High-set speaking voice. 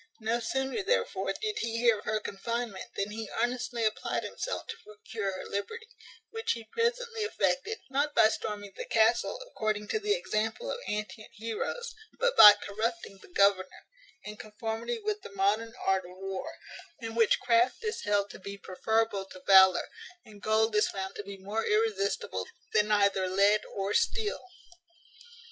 Yes: high, 220 Hz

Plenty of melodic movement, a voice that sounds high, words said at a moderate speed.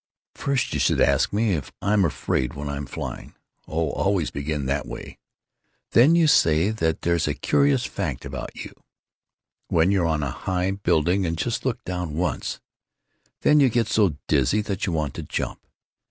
No: wide, 5.9 semitones; very low, 90 Hz; average, 170 wpm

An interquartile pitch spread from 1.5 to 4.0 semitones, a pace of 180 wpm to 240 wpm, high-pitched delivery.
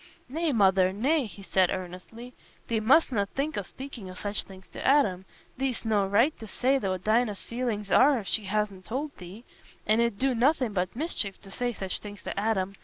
No: average, 4.6 semitones; average, 200 wpm; high, 215 Hz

